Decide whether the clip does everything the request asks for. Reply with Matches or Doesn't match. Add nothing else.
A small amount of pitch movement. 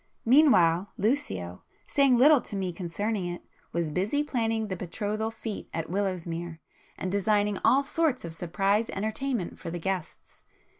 Doesn't match